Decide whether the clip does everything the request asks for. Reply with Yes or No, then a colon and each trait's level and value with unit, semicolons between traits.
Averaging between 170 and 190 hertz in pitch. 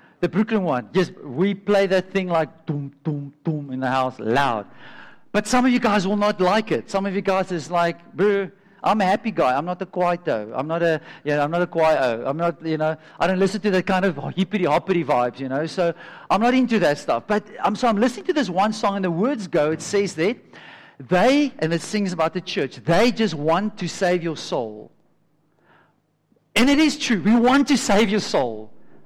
Yes: medium, 185 Hz